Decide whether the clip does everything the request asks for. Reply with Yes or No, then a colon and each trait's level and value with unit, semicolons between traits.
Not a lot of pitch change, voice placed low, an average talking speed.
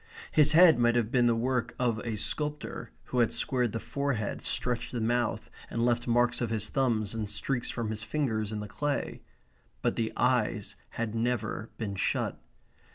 Yes: narrow, 2.2 semitones; low, 120 Hz; average, 180 wpm